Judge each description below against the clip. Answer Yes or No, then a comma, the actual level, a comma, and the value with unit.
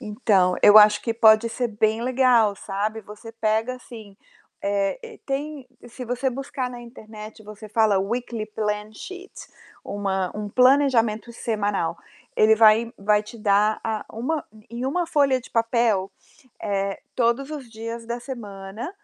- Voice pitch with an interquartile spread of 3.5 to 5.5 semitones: No, average, 2.9 semitones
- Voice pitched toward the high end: Yes, high, 225 Hz